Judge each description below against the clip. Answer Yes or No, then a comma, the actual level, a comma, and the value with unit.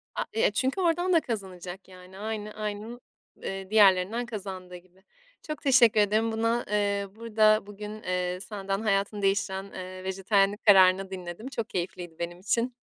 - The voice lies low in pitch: No, high, 200 Hz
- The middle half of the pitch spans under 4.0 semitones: Yes, average, 2.8 semitones